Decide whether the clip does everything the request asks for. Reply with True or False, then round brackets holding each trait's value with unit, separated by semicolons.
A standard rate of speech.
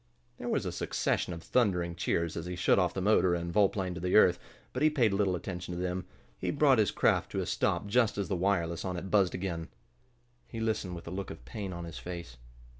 False (230 wpm)